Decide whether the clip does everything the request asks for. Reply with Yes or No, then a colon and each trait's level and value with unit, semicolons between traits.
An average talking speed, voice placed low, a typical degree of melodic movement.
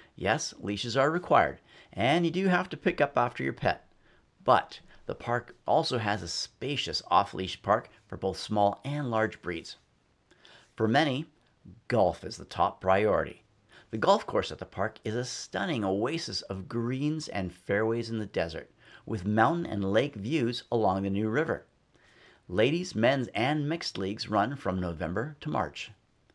No: average, 165 wpm; low, 110 Hz; wide, 6.6 semitones